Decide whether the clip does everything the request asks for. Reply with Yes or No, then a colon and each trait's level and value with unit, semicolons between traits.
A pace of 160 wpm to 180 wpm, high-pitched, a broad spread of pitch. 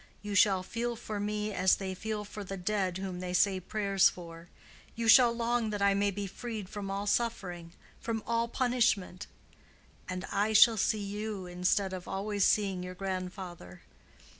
No: average, 165 wpm; high, 200 Hz; average, 2.8 semitones